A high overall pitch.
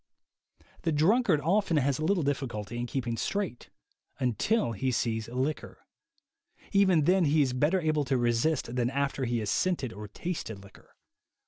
No: medium, 140 Hz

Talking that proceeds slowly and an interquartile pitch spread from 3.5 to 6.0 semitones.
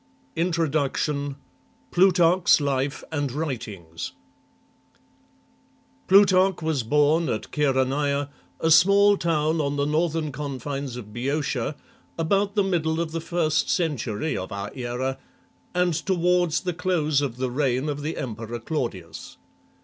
Yes: slow, 120 wpm; average, 4.0 semitones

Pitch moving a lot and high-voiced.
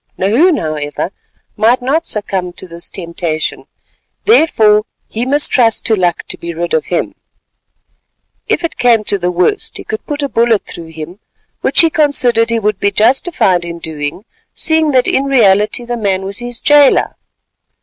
Yes: wide, 6.7 semitones; high, 215 Hz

